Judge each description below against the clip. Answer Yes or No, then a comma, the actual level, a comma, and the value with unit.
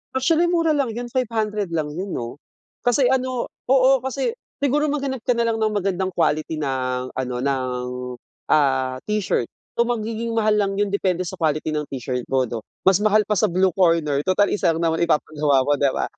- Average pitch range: No, wide, 7.9 semitones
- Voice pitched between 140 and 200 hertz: Yes, high, 190 Hz